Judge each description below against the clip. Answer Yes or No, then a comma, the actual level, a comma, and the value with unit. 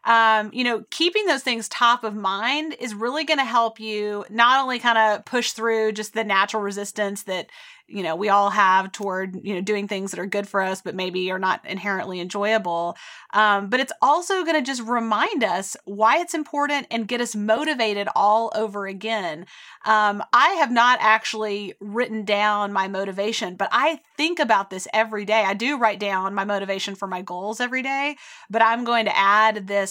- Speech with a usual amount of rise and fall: Yes, average, 3.2 semitones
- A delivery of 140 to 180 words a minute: No, average, 200 wpm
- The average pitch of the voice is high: Yes, high, 215 Hz